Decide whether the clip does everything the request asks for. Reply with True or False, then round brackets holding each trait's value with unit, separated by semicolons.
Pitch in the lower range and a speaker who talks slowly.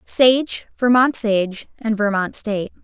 False (220 Hz; 125 wpm)